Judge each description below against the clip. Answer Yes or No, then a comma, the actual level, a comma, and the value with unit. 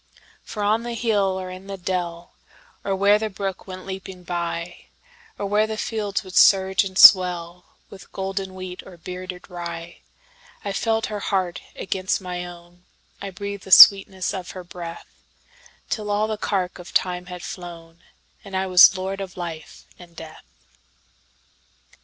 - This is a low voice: No, high, 190 Hz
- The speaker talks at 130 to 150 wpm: Yes, average, 140 wpm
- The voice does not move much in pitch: Yes, narrow, 2.1 semitones